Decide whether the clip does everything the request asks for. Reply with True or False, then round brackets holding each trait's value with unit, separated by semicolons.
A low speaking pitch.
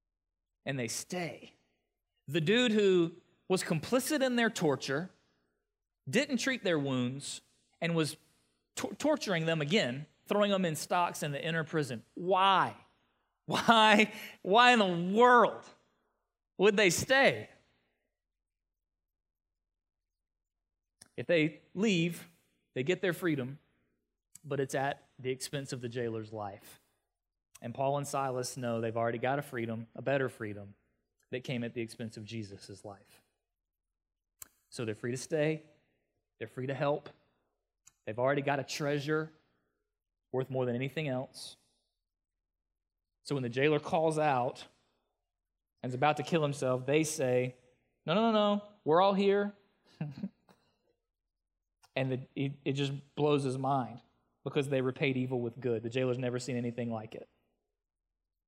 True (130 Hz)